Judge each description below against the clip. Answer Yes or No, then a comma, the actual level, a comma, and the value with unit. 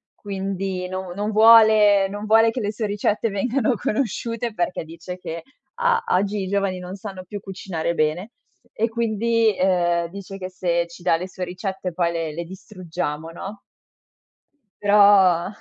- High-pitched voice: Yes, high, 195 Hz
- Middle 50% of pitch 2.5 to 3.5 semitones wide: Yes, average, 2.8 semitones